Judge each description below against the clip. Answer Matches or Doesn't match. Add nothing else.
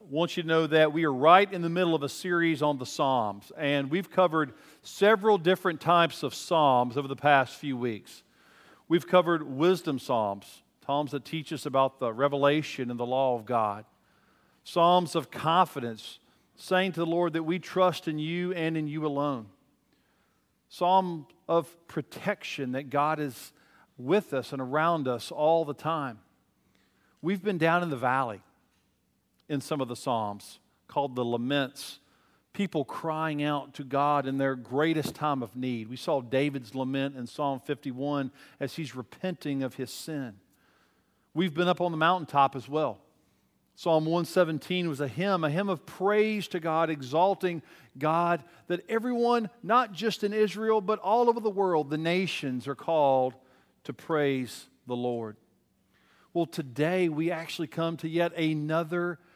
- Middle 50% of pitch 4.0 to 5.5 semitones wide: Matches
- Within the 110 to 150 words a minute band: Doesn't match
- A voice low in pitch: Doesn't match